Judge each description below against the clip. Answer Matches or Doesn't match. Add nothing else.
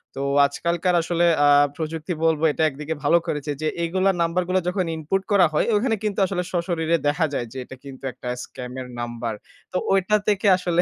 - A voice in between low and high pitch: Matches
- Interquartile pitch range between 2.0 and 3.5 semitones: Doesn't match